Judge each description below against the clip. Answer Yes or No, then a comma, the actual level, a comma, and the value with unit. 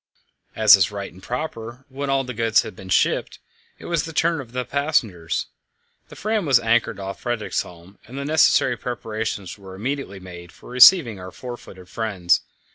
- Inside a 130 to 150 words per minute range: No, average, 180 wpm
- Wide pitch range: Yes, wide, 5.7 semitones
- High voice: No, low, 115 Hz